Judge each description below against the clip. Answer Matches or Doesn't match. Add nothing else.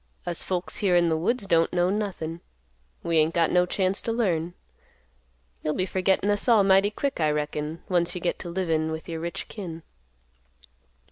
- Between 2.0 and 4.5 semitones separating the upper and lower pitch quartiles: Matches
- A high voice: Doesn't match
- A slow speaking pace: Doesn't match